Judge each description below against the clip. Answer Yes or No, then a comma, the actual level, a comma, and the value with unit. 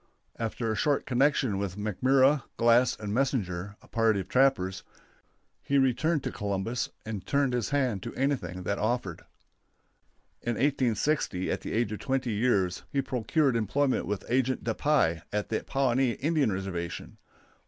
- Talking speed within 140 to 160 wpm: Yes, average, 155 wpm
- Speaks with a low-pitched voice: Yes, low, 120 Hz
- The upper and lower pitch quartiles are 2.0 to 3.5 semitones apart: No, average, 4.9 semitones